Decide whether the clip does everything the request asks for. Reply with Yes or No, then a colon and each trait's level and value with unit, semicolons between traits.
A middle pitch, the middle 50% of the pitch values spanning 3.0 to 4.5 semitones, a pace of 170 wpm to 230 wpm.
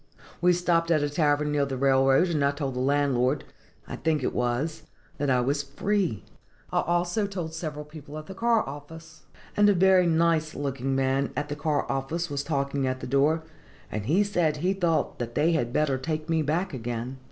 Yes: medium, 150 Hz; average, 3.6 semitones; average, 200 wpm